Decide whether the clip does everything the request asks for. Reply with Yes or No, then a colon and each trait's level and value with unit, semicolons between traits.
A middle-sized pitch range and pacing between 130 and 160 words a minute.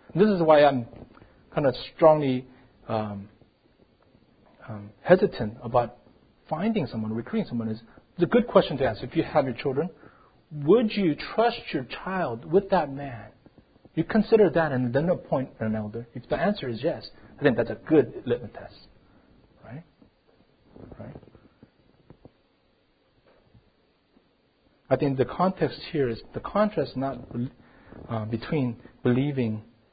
No: wide, 6.4 semitones; slow, 135 wpm